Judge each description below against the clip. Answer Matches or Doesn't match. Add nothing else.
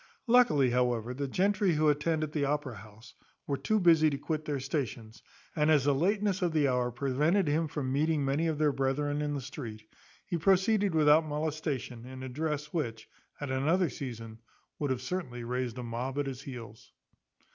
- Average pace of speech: Matches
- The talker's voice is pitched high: Doesn't match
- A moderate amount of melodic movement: Matches